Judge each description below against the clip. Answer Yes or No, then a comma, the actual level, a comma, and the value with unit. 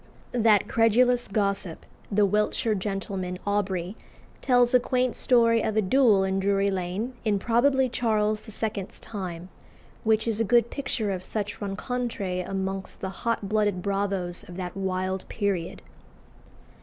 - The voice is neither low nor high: No, high, 205 Hz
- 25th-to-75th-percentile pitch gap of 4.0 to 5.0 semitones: No, average, 3.1 semitones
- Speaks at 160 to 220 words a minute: No, average, 140 wpm